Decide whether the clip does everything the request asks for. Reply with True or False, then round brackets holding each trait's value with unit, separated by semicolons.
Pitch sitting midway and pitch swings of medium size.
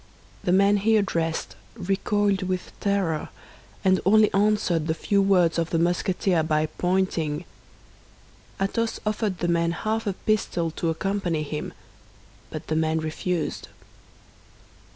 True (180 Hz; 3.5 semitones)